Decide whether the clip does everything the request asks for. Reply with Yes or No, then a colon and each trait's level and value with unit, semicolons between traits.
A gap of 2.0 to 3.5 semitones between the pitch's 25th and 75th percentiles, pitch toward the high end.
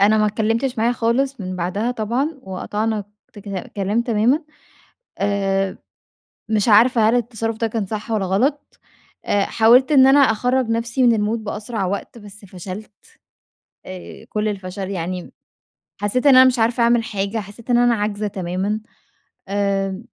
Yes: average, 2.9 semitones; high, 215 Hz